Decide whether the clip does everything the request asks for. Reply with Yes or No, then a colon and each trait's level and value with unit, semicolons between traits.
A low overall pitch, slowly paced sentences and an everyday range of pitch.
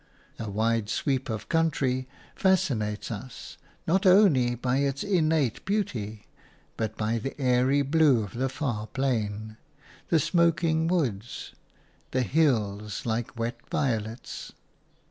No: low, 130 Hz; slow, 120 wpm; wide, 5.9 semitones